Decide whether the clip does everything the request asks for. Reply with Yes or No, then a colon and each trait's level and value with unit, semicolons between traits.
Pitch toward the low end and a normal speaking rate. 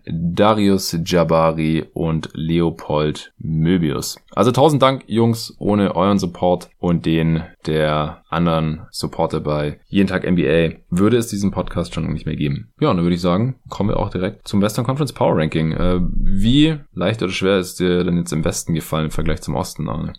Yes: very low, 90 Hz; average, 180 wpm